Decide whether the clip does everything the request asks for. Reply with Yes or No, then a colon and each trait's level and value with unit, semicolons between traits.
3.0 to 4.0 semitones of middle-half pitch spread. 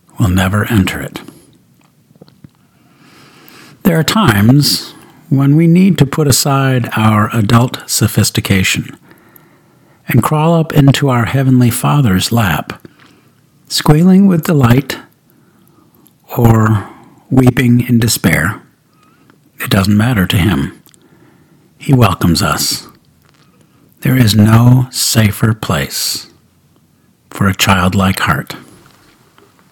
No: average, 5.1 semitones